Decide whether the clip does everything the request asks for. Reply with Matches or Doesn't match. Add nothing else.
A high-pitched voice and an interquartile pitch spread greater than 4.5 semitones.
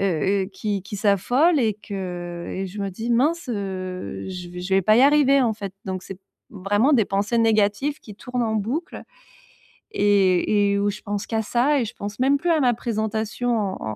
Doesn't match